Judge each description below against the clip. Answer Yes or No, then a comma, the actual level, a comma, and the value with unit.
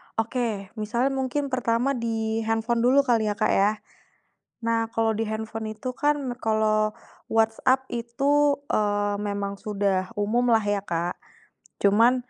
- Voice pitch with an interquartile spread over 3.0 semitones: No, average, 2.7 semitones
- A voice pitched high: Yes, high, 225 Hz